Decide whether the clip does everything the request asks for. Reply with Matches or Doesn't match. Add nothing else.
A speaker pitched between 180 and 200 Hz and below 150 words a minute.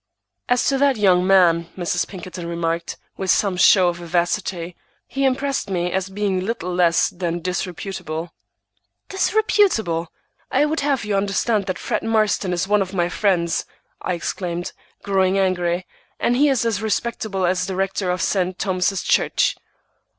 Doesn't match